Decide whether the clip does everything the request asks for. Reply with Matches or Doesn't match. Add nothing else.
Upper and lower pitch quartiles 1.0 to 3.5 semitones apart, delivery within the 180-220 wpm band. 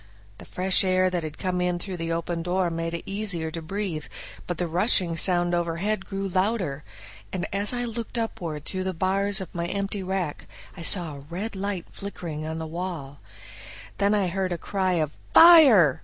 Matches